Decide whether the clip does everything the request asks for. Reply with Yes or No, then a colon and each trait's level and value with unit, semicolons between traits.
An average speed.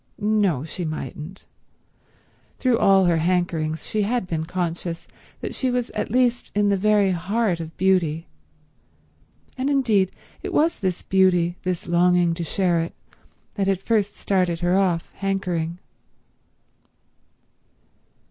No: slow, 130 wpm